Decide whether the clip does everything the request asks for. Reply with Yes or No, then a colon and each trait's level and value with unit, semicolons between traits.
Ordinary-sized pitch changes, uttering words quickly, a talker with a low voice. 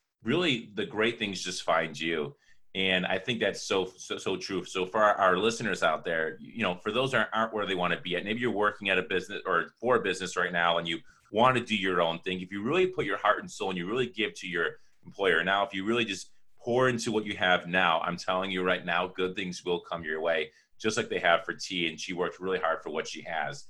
Yes: average, 3.3 semitones; fast, 270 wpm; very low, 95 Hz